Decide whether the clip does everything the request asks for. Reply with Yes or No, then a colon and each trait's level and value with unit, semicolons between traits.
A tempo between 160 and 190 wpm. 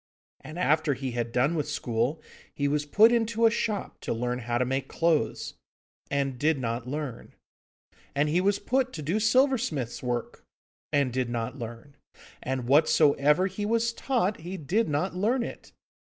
Yes: average, 170 wpm